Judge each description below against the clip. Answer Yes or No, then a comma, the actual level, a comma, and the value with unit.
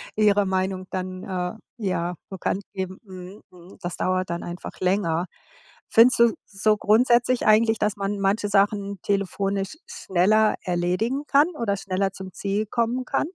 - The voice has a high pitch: Yes, high, 195 Hz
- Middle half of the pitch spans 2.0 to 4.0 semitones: Yes, narrow, 2.5 semitones